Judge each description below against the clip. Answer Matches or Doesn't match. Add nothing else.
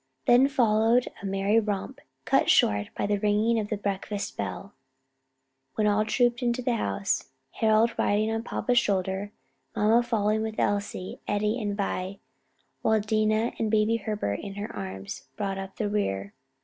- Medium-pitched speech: Doesn't match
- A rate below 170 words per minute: Matches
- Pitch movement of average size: Doesn't match